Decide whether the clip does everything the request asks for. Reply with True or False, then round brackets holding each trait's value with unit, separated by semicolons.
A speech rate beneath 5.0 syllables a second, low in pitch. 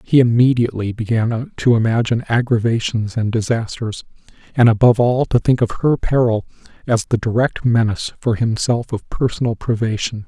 False (5.4 syllables/s; 115 Hz)